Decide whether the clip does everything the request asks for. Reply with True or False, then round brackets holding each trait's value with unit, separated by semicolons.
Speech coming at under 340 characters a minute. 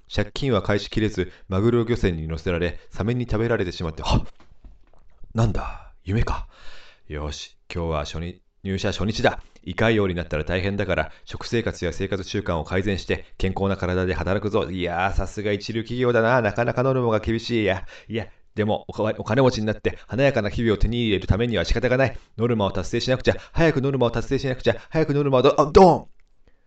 False (395 characters per minute)